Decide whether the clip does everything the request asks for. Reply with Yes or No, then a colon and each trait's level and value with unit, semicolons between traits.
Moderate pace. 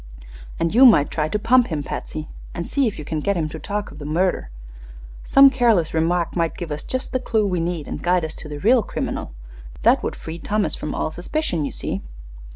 No: fast, 225 wpm